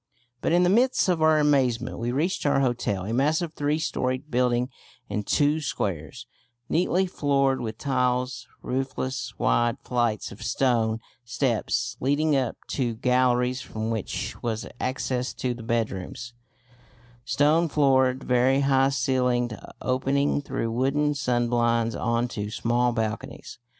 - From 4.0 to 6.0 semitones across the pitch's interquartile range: No, average, 2.8 semitones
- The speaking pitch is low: Yes, low, 125 Hz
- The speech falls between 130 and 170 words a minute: Yes, slow, 135 wpm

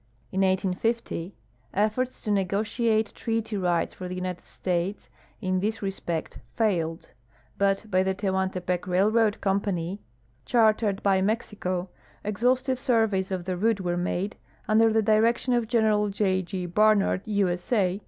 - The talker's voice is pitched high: Yes, high, 200 Hz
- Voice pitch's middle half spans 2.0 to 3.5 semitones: Yes, average, 2.9 semitones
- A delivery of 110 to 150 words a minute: Yes, average, 145 wpm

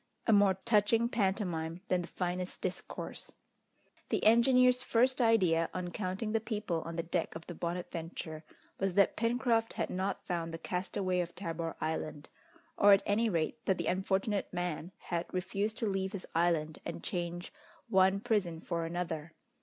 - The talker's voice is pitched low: No, medium, 185 Hz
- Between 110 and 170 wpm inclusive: Yes, average, 160 wpm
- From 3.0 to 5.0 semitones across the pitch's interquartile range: Yes, average, 3.6 semitones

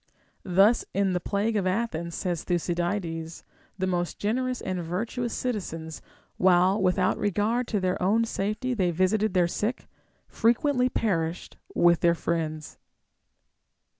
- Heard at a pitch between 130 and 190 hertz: Yes, medium, 185 Hz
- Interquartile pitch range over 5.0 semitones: No, average, 4.1 semitones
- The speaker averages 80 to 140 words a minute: Yes, slow, 135 wpm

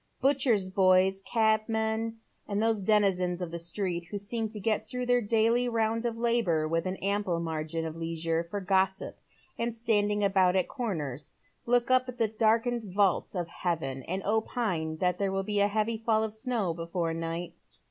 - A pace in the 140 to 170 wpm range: No, average, 180 wpm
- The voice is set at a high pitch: Yes, high, 200 Hz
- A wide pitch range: No, average, 4.3 semitones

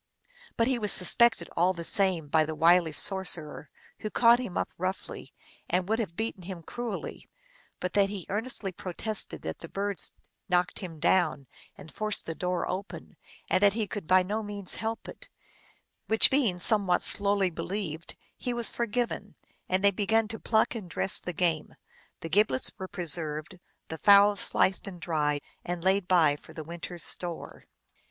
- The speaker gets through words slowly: No, average, 175 wpm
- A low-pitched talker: No, high, 190 Hz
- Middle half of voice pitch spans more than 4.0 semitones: No, average, 3.6 semitones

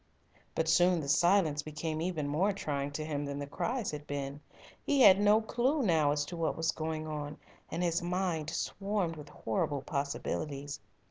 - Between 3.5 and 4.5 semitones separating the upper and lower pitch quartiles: Yes, average, 3.8 semitones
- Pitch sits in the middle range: Yes, medium, 160 Hz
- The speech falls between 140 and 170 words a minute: No, average, 180 wpm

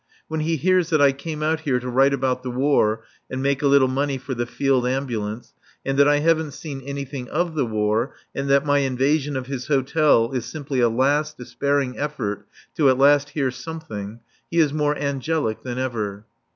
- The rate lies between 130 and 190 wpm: No, average, 200 wpm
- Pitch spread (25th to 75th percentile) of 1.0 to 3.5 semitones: Yes, average, 2.8 semitones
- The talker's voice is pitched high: No, low, 135 Hz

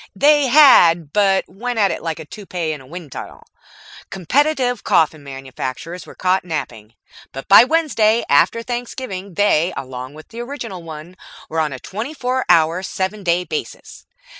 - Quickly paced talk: No, average, 160 wpm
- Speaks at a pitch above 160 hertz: Yes, medium, 185 Hz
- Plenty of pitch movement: Yes, wide, 7.2 semitones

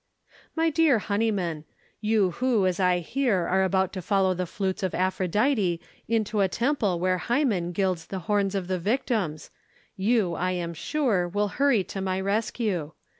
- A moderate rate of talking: Yes, average, 165 wpm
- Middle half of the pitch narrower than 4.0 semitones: Yes, average, 3.5 semitones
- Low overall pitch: No, high, 195 Hz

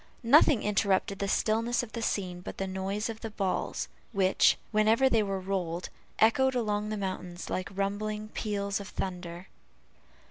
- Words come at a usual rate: Yes, average, 155 wpm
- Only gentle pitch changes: Yes, narrow, 2.3 semitones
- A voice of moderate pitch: No, high, 200 Hz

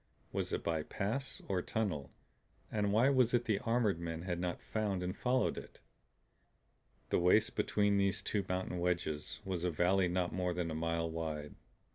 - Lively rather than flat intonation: No, average, 3.7 semitones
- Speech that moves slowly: No, average, 175 wpm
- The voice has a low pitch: Yes, very low, 90 Hz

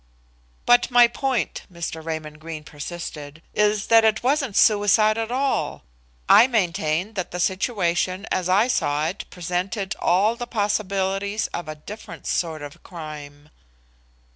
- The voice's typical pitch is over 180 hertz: Yes, high, 190 Hz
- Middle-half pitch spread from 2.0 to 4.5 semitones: No, average, 5.2 semitones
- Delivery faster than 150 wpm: No, average, 140 wpm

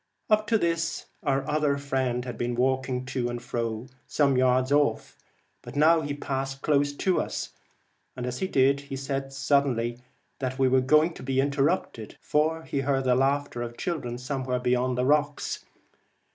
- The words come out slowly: No, average, 175 wpm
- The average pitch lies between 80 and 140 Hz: Yes, low, 135 Hz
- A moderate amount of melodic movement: No, narrow, 2.3 semitones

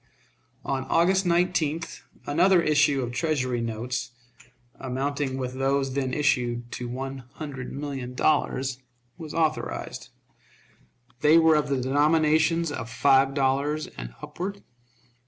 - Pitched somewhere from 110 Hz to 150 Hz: Yes, medium, 140 Hz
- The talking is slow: Yes, slow, 120 wpm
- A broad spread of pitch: No, average, 3.3 semitones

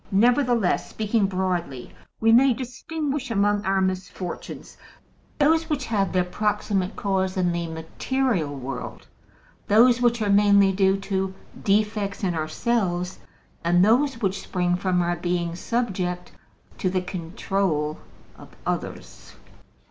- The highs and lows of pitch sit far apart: No, average, 4.1 semitones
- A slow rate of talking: Yes, slow, 125 wpm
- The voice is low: No, high, 195 Hz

